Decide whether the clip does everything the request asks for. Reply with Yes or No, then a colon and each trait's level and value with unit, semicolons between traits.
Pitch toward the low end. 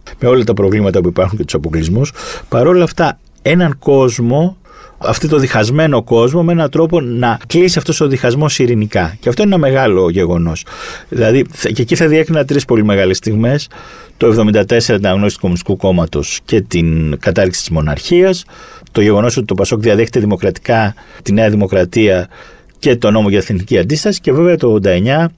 Yes: low, 120 Hz